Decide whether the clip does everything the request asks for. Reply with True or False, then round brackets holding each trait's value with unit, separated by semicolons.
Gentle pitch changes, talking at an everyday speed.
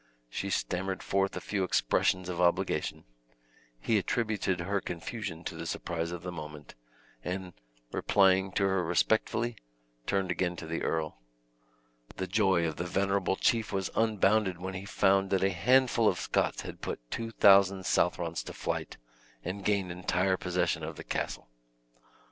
True (2.1 semitones; 155 wpm)